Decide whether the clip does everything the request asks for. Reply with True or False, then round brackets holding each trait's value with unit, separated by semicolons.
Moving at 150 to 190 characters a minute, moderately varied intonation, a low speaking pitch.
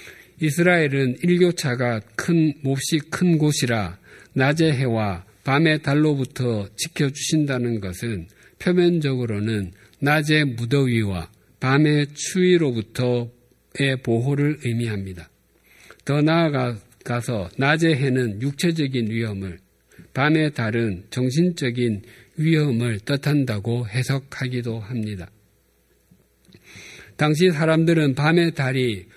False (230 characters per minute; 4.9 semitones; 130 Hz)